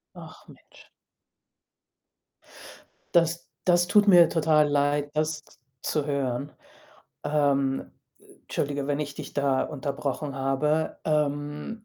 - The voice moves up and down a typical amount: No, narrow, 1.8 semitones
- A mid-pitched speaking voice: Yes, medium, 145 Hz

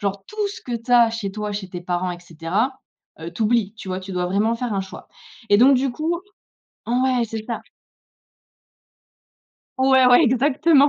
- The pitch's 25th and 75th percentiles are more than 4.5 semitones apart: Yes, average, 5.1 semitones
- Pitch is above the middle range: Yes, high, 225 Hz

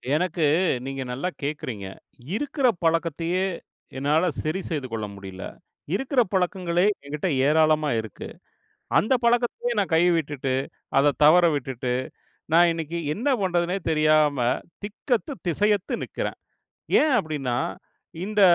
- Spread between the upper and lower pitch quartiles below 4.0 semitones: No, average, 4.8 semitones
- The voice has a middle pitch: Yes, medium, 165 Hz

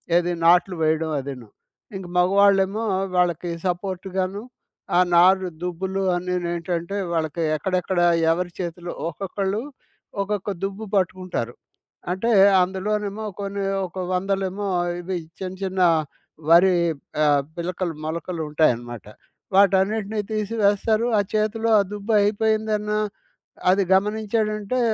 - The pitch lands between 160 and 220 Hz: Yes, high, 190 Hz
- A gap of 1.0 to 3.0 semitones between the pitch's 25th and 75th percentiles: Yes, narrow, 2.6 semitones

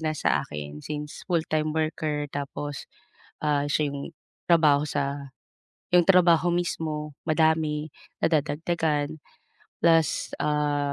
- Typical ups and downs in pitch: No, narrow, 1.9 semitones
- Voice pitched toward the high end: No, medium, 150 Hz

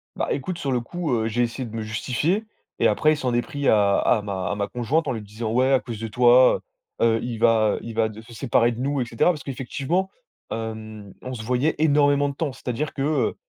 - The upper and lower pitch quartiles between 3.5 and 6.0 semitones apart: Yes, average, 4.0 semitones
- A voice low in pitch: Yes, low, 120 Hz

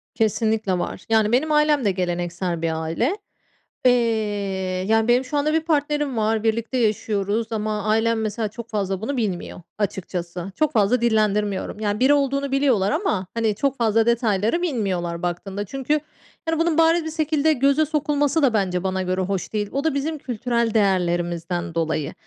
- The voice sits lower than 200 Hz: No, high, 220 Hz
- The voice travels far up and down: Yes, wide, 6.3 semitones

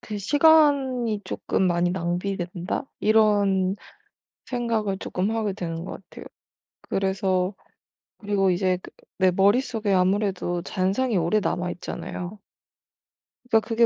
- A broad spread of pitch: No, average, 3.2 semitones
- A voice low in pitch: No, high, 195 Hz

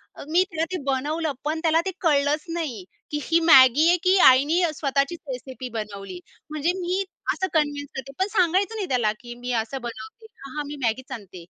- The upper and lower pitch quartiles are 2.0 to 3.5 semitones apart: No, average, 4.6 semitones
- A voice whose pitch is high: Yes, very high, 290 Hz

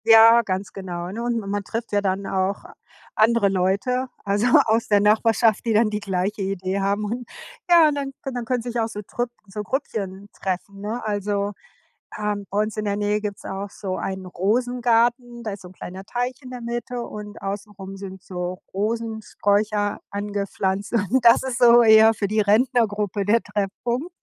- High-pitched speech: Yes, high, 210 Hz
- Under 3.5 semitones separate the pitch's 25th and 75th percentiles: Yes, average, 2.9 semitones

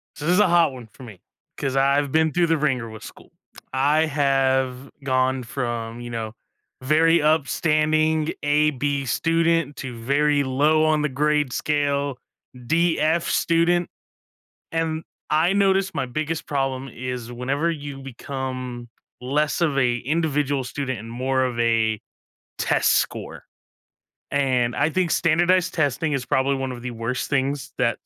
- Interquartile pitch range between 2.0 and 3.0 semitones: No, average, 3.4 semitones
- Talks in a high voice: No, medium, 140 Hz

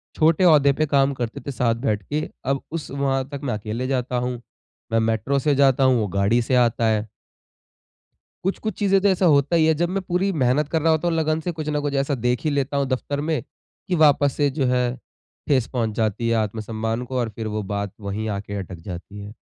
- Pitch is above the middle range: No, low, 130 Hz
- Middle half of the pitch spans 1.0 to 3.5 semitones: No, average, 4.9 semitones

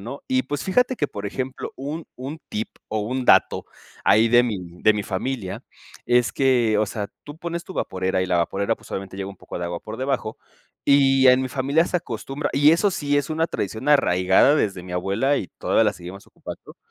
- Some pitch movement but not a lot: No, wide, 6.3 semitones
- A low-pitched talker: Yes, low, 125 Hz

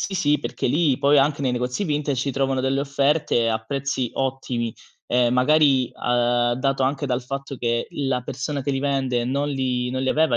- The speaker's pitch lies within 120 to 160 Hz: Yes, low, 135 Hz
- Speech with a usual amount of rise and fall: No, narrow, 2.2 semitones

